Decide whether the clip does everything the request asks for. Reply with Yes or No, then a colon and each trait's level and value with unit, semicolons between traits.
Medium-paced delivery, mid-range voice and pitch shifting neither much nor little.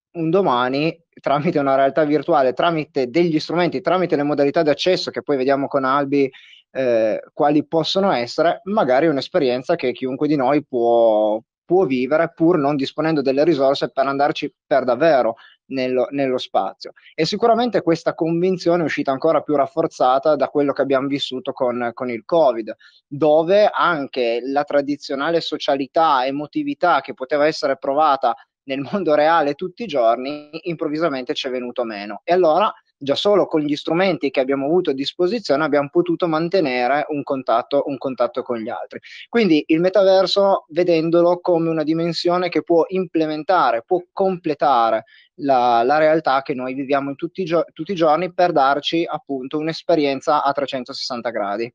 Yes: average, 160 wpm; medium, 150 Hz; average, 3.6 semitones